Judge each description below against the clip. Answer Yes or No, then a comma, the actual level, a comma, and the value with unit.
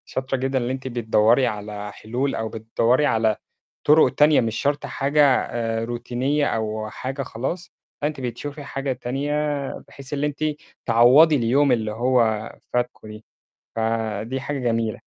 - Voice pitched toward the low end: Yes, low, 125 Hz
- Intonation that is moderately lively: Yes, average, 3.6 semitones